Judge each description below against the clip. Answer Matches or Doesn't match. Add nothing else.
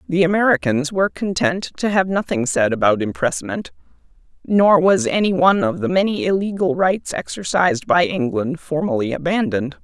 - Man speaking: Doesn't match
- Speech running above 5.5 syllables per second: Doesn't match